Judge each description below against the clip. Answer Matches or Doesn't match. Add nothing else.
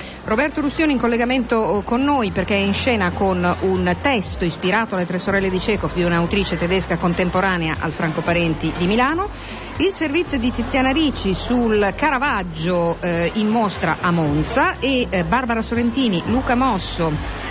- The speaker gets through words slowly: Doesn't match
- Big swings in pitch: Matches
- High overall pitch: Matches